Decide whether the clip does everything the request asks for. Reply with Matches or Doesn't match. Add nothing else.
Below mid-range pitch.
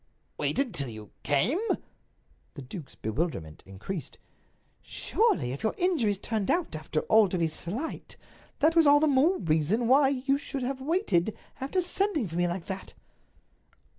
Doesn't match